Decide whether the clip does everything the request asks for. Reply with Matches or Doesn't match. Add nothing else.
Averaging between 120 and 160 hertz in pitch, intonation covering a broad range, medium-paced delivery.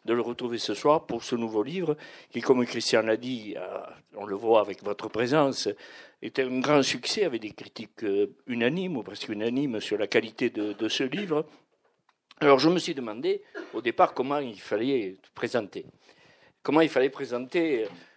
Matches